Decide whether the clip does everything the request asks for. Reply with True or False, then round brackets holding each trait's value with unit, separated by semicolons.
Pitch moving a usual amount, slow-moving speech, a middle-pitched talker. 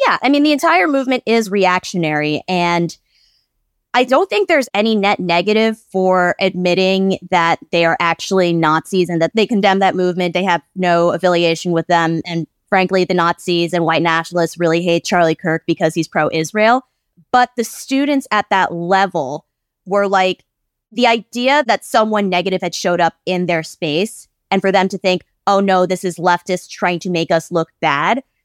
False (3.3 semitones; 180 wpm; 180 Hz)